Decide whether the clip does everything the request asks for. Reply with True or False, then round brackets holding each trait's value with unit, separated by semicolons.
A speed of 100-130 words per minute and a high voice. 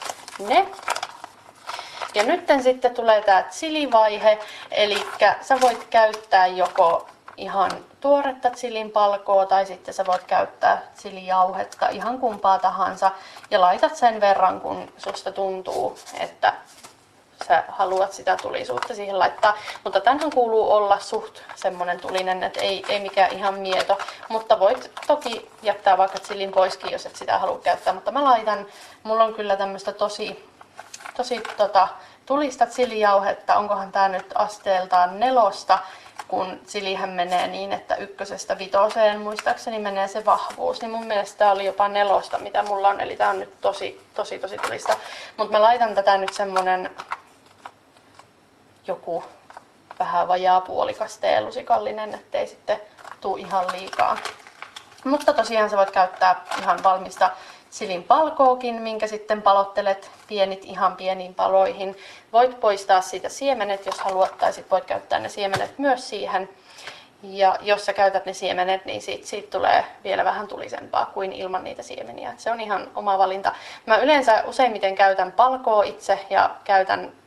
False (145 wpm; 205 Hz)